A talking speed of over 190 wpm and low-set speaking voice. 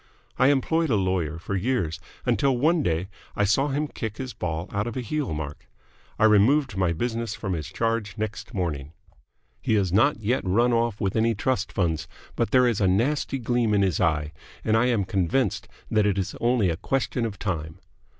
Yes: average, 200 wpm; low, 105 Hz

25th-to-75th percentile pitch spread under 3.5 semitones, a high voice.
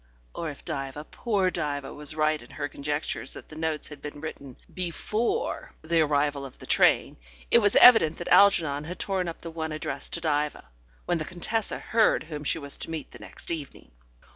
No: average, 2.9 semitones; medium, 155 Hz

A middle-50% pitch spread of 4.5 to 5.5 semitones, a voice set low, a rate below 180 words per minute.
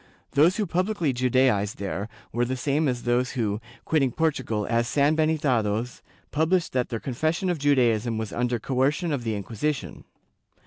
Yes: average, 4.8 semitones; low, 130 Hz; average, 150 wpm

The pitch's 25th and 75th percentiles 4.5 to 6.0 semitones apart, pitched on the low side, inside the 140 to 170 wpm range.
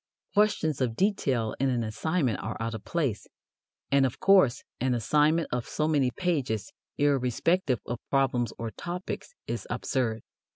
Yes: average, 5.3 semitones; low, 130 Hz; average, 150 wpm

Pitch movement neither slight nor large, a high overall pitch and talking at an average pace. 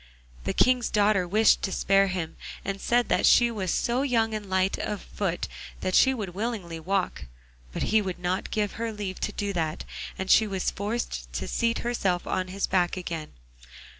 Yes: average, 3.3 semitones; high, 195 Hz; average, 190 wpm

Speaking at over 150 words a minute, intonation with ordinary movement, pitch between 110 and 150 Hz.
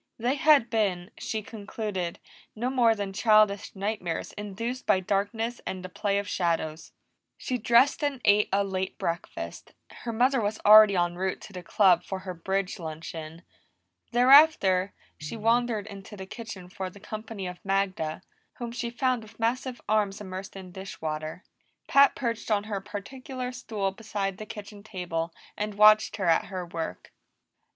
No: average, 160 wpm; average, 3.5 semitones; high, 205 Hz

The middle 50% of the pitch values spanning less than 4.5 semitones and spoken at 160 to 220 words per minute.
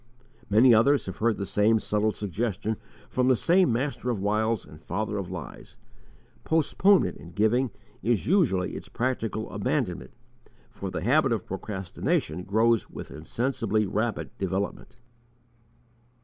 No: average, 4.0 semitones; slow, 135 wpm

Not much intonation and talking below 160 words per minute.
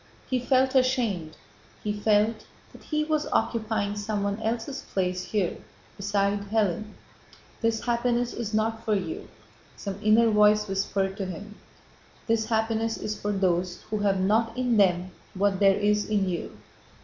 Yes: narrow, 2.3 semitones; average, 150 wpm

